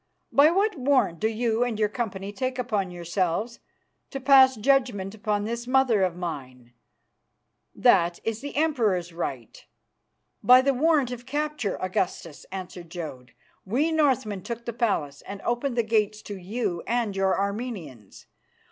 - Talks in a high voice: Yes, high, 220 Hz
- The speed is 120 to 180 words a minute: Yes, average, 145 wpm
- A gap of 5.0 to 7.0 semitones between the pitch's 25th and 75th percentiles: Yes, wide, 5.5 semitones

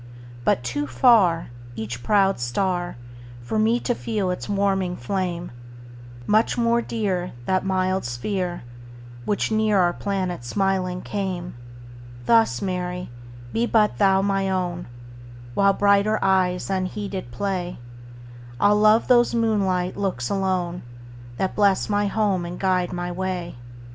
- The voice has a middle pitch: Yes, medium, 180 Hz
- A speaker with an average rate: No, slow, 105 wpm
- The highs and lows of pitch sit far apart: Yes, wide, 8.6 semitones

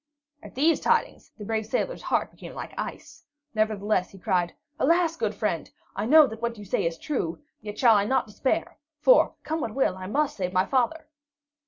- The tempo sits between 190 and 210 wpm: Yes, average, 195 wpm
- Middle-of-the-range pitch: No, high, 220 Hz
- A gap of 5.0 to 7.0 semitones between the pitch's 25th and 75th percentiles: Yes, wide, 5.4 semitones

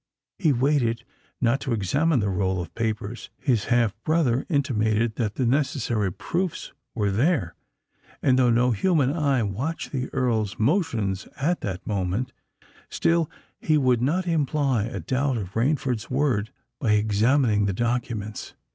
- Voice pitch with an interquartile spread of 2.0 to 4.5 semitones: No, average, 4.9 semitones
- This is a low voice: Yes, low, 120 Hz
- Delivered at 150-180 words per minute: No, average, 140 wpm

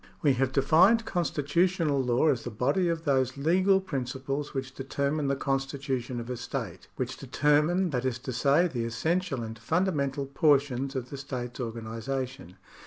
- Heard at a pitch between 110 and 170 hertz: Yes, low, 135 Hz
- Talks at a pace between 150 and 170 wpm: Yes, average, 165 wpm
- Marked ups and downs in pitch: No, average, 3.3 semitones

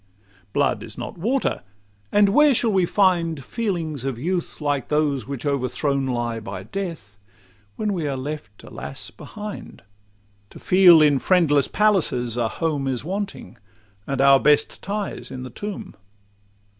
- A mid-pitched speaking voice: Yes, medium, 150 Hz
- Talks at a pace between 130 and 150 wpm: Yes, average, 145 wpm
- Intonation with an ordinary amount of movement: No, wide, 6.4 semitones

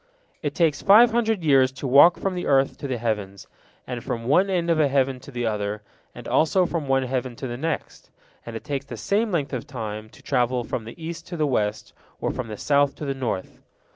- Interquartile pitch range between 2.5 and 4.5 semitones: No, average, 5.1 semitones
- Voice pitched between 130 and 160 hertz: Yes, low, 135 Hz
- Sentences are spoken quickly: Yes, fast, 230 wpm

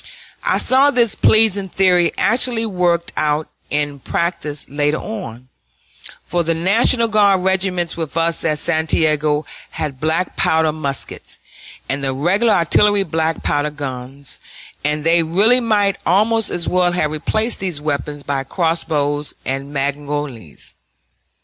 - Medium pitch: Yes, medium, 165 Hz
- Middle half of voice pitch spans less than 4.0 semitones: No, average, 4.7 semitones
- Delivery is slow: Yes, slow, 130 wpm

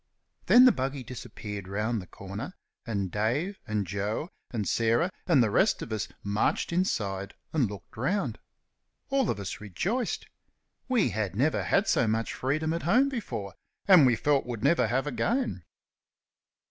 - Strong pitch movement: Yes, wide, 8.6 semitones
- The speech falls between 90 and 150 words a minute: No, average, 160 wpm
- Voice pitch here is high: No, low, 120 Hz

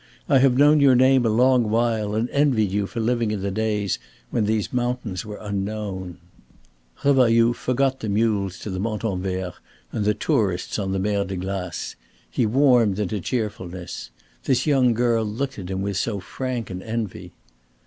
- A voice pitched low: Yes, low, 110 Hz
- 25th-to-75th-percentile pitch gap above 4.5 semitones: No, average, 3.9 semitones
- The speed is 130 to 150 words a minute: No, average, 170 wpm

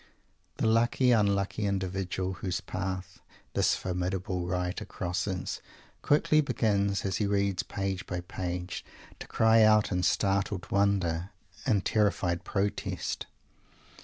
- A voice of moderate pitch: No, very low, 95 Hz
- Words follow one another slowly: Yes, slow, 115 wpm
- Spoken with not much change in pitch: Yes, narrow, 2.1 semitones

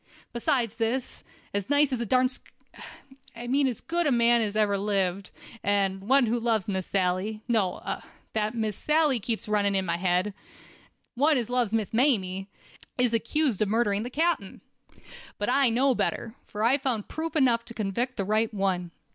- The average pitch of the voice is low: No, high, 225 Hz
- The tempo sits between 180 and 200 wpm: No, average, 165 wpm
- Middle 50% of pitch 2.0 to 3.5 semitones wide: No, average, 4.0 semitones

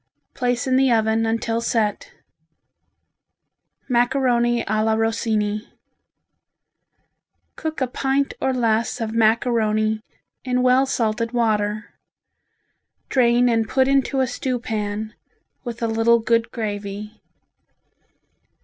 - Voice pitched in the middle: No, high, 230 Hz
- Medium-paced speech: No, slow, 105 wpm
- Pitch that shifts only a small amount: Yes, narrow, 2.3 semitones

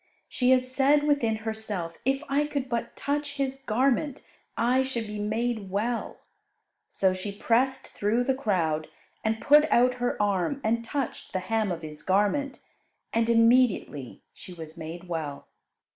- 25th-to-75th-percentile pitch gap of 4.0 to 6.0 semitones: Yes, average, 5.1 semitones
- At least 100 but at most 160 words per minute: Yes, average, 155 wpm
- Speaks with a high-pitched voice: Yes, high, 230 Hz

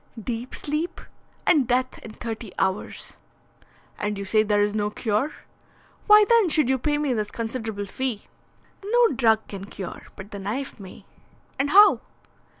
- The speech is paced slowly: No, average, 155 wpm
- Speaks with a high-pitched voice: Yes, high, 230 Hz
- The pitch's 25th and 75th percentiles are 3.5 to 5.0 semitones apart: No, wide, 5.5 semitones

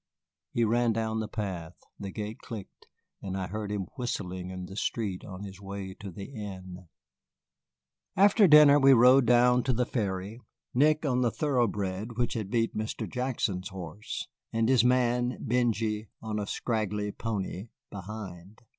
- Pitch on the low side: Yes, low, 110 Hz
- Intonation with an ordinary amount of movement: Yes, average, 4.0 semitones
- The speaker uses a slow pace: No, average, 155 wpm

